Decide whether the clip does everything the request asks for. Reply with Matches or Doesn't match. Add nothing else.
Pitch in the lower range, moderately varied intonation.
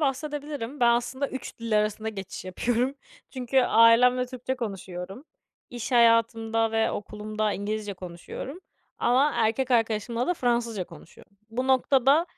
Doesn't match